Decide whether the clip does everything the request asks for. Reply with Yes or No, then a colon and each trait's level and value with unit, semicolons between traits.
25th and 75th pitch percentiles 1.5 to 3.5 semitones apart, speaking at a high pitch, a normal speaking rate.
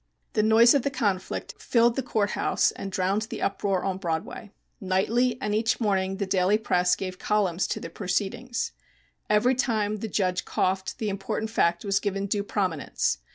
Yes: average, 2.7 semitones; high, 200 Hz; average, 175 wpm